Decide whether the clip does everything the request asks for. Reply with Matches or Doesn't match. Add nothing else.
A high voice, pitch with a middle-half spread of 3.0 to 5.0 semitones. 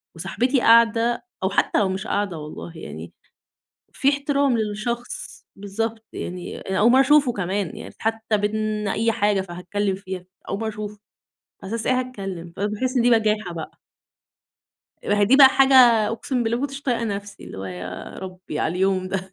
Matches